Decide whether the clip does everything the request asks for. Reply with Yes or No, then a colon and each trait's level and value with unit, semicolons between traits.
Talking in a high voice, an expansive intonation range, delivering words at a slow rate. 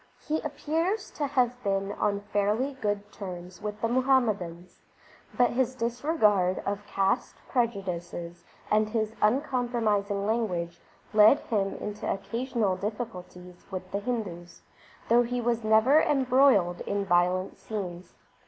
No: high, 210 Hz; average, 4.2 semitones; slow, 120 wpm